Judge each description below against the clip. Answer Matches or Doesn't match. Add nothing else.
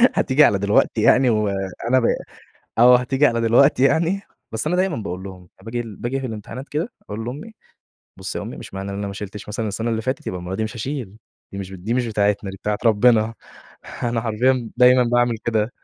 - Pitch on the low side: Matches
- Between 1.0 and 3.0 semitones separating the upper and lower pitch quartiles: Doesn't match